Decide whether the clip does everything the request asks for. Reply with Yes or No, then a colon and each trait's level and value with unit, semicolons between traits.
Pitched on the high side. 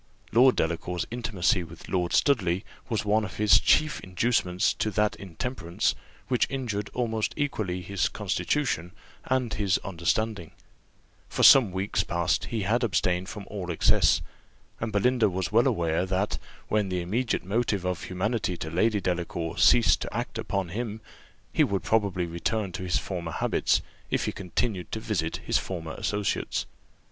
No: low, 100 Hz